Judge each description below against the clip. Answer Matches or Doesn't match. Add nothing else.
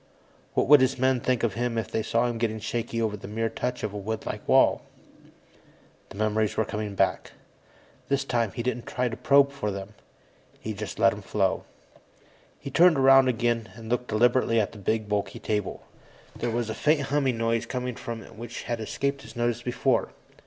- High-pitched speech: Doesn't match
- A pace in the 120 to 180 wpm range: Doesn't match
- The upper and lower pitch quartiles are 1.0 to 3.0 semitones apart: Matches